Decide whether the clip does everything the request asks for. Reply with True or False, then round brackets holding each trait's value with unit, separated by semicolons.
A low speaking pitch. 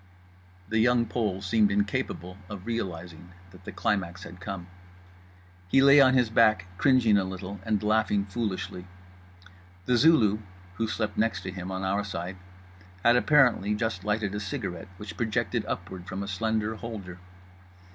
True (105 Hz)